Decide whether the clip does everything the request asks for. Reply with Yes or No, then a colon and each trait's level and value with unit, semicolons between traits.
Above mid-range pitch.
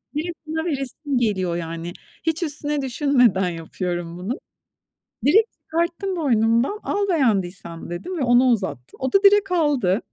Yes: very high, 260 Hz